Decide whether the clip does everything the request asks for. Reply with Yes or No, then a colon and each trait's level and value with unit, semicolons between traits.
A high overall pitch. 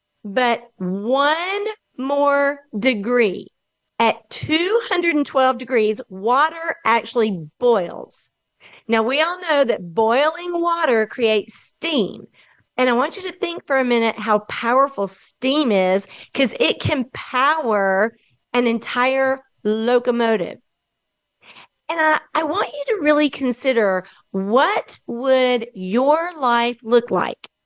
Yes: very high, 250 Hz